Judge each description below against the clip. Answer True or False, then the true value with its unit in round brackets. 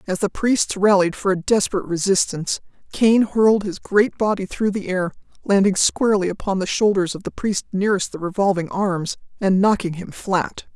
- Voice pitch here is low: False (195 Hz)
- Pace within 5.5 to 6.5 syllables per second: False (5.3 syllables/s)